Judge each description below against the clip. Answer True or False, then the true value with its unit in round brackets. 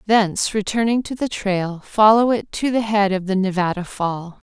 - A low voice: False (205 Hz)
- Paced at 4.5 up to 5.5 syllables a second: True (4.8 syllables/s)